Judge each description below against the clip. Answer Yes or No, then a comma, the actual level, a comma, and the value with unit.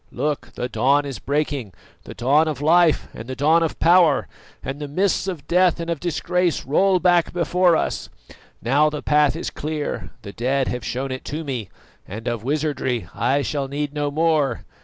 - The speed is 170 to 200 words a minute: Yes, average, 185 wpm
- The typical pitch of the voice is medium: Yes, medium, 145 Hz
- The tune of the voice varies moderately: Yes, average, 3.7 semitones